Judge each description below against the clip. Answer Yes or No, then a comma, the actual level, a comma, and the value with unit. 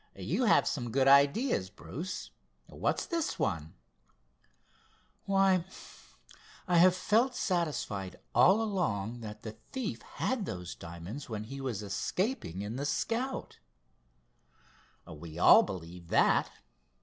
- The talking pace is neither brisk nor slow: No, slow, 115 wpm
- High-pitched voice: No, low, 135 Hz